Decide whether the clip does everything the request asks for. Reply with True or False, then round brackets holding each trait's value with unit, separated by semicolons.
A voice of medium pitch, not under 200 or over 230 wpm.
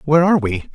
False (145 Hz; 240 wpm)